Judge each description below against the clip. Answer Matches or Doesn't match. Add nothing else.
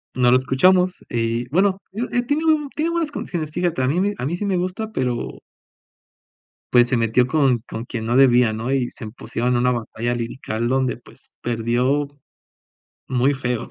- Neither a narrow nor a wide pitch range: Doesn't match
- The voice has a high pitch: Doesn't match